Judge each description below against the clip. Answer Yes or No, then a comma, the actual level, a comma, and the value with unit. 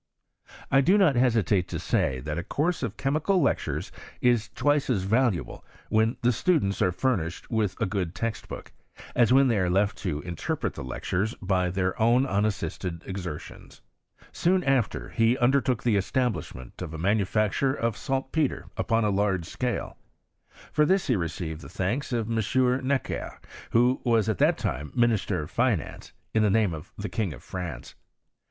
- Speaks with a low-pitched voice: Yes, low, 110 Hz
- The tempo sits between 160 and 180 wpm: Yes, average, 170 wpm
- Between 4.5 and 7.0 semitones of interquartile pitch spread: Yes, wide, 5.6 semitones